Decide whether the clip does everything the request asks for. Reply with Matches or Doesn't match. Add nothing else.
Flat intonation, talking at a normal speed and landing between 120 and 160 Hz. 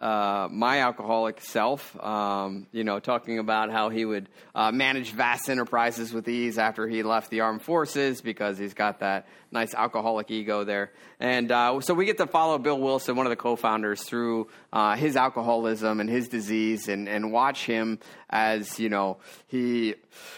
Doesn't match